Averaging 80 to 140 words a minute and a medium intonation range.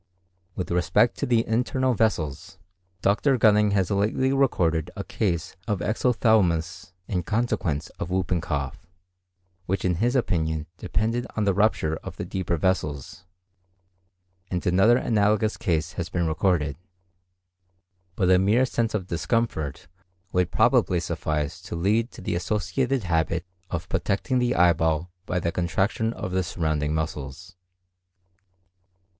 Yes: slow, 135 wpm; average, 4.9 semitones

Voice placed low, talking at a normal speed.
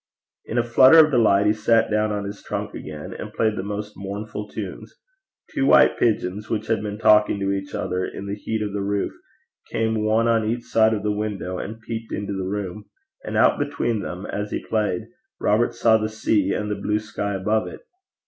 No: low, 105 Hz; fast, 215 wpm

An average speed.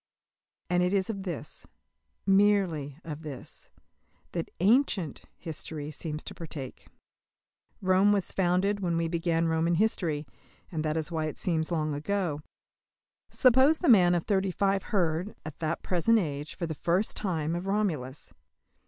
Yes: average, 150 wpm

